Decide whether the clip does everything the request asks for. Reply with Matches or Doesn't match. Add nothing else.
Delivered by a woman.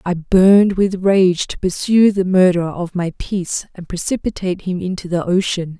Matches